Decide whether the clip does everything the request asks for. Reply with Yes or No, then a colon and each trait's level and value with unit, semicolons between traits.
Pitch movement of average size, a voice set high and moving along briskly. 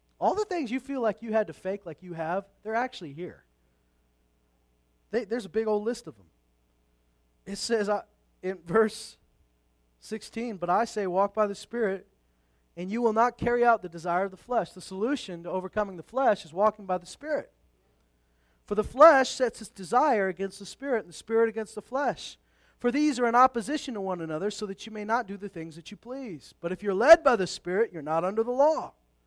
No: wide, 6.4 semitones; high, 200 Hz; fast, 215 wpm